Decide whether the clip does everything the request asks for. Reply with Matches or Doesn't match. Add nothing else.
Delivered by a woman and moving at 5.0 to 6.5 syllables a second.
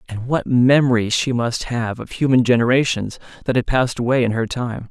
Doesn't match